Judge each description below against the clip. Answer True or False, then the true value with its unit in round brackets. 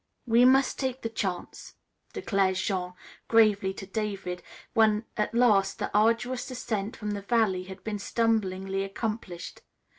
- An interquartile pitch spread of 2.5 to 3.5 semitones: True (2.9 semitones)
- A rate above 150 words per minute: False (140 wpm)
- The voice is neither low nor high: False (210 Hz)